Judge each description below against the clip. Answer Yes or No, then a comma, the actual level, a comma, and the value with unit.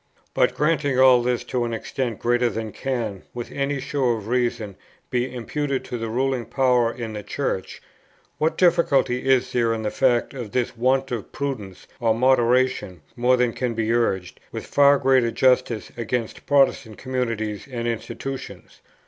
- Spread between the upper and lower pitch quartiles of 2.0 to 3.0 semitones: Yes, narrow, 2.4 semitones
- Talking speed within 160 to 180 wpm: Yes, average, 165 wpm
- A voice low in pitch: Yes, low, 125 Hz